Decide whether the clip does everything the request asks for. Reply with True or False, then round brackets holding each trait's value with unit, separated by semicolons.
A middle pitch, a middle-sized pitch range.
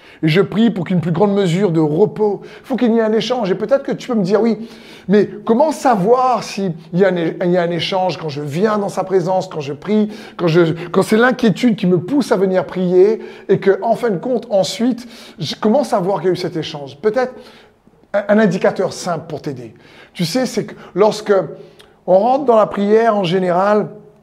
False (200 Hz; 3.3 semitones)